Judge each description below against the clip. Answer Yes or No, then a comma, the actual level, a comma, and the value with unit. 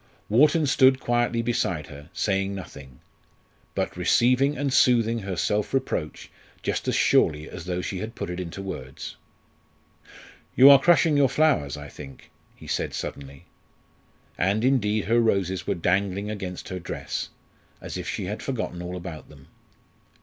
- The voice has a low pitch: Yes, low, 100 Hz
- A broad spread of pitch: Yes, wide, 5.7 semitones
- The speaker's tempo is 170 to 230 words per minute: No, average, 155 wpm